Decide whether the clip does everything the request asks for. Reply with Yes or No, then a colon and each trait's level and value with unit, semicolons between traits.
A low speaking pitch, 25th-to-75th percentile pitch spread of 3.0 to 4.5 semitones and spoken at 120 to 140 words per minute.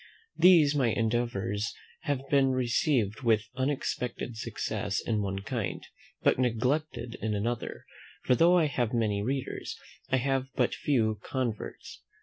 Yes: low, 120 Hz; average, 3.6 semitones; slow, 135 wpm